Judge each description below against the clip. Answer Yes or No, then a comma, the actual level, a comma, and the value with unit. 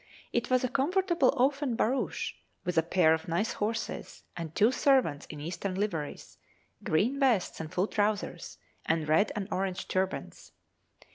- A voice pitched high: Yes, high, 205 Hz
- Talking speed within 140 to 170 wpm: Yes, average, 150 wpm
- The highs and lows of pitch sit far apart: Yes, wide, 7.2 semitones